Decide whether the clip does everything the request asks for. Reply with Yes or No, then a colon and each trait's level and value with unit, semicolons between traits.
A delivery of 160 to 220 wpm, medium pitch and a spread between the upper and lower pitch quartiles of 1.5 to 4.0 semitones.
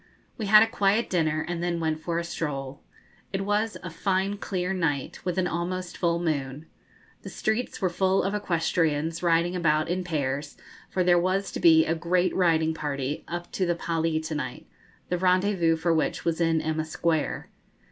Yes: average, 185 wpm; medium, 170 Hz; narrow, 2.6 semitones